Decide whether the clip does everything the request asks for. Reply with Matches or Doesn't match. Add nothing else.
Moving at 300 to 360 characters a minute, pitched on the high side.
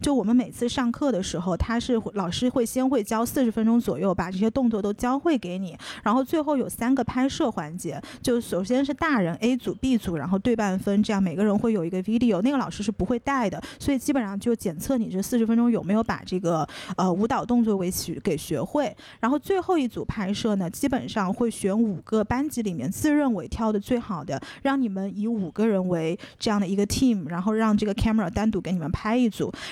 Matches